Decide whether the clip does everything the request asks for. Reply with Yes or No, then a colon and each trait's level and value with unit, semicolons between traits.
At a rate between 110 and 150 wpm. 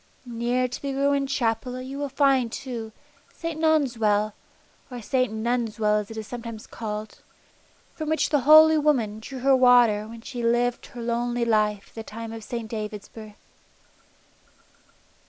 No: average, 165 wpm